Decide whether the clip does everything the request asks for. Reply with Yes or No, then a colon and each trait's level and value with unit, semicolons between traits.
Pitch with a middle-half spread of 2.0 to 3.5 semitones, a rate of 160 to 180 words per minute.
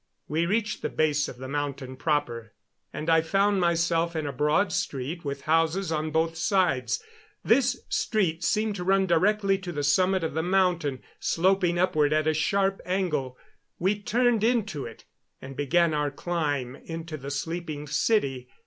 No: average, 4.6 semitones; average, 165 wpm